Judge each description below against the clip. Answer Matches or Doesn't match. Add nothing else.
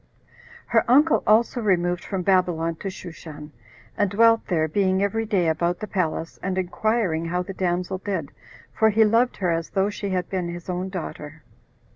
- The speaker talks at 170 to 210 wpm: Matches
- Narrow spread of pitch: Doesn't match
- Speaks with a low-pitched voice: Doesn't match